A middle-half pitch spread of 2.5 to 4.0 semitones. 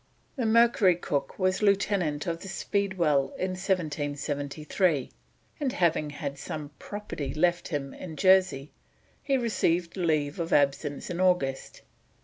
No: average, 4.6 semitones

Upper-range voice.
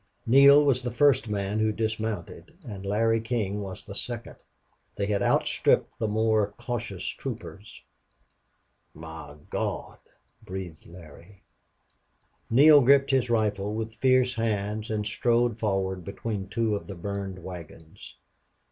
No: low, 110 Hz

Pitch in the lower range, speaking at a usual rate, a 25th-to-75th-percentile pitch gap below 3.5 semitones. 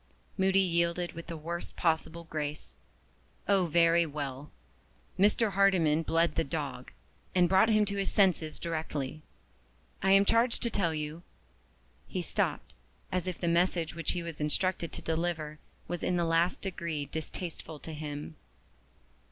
No: medium, 170 Hz; average, 155 wpm; average, 2.9 semitones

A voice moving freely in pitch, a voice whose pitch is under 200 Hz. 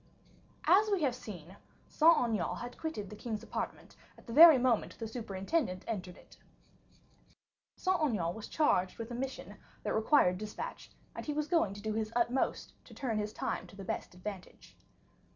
No: wide, 5.8 semitones; high, 225 Hz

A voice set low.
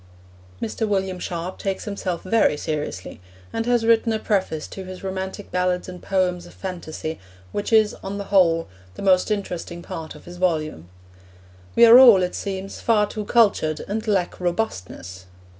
No: high, 190 Hz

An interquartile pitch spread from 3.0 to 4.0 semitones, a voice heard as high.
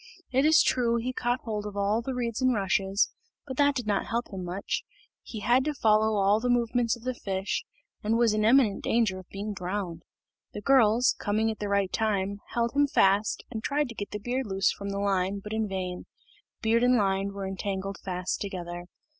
Yes: average, 3.4 semitones; high, 210 Hz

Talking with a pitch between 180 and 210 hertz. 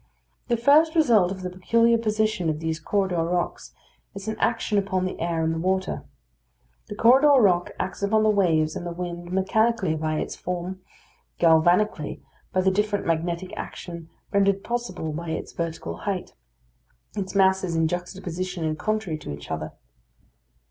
Yes: medium, 185 Hz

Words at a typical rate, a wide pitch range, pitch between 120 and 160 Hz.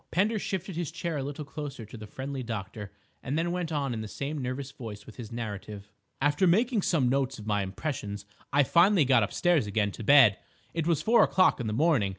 No: fast, 215 wpm; wide, 7.1 semitones; low, 135 Hz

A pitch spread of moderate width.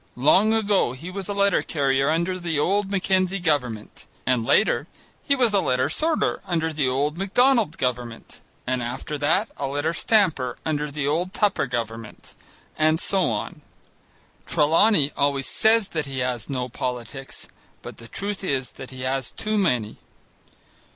No: wide, 7.0 semitones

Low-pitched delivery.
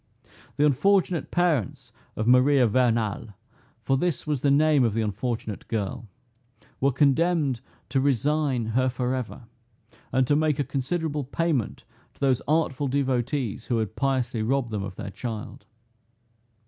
Yes: low, 130 Hz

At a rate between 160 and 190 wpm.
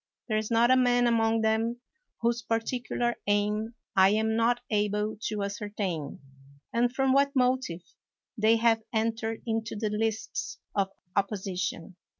No: average, 145 wpm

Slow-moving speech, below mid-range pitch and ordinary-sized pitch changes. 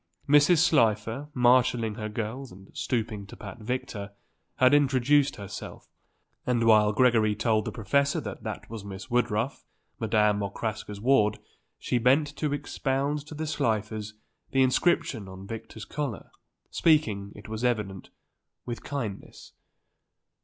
Yes: slow, 130 wpm; low, 115 Hz; average, 4.3 semitones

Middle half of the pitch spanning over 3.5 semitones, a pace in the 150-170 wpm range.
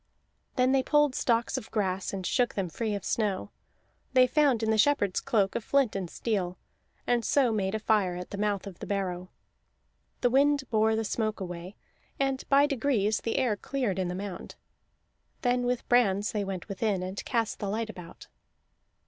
No: average, 4.2 semitones; average, 185 wpm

